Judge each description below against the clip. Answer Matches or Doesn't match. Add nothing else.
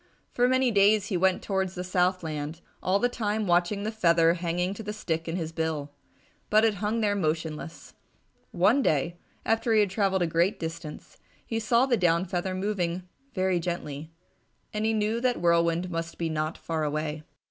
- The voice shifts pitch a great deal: Doesn't match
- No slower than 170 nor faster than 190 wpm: Matches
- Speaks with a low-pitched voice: Doesn't match